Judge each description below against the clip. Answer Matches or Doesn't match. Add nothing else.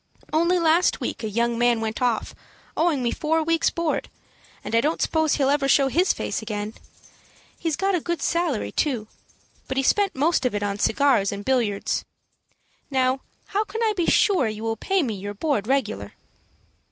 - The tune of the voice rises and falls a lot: Matches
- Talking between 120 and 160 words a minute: Doesn't match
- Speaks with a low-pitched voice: Doesn't match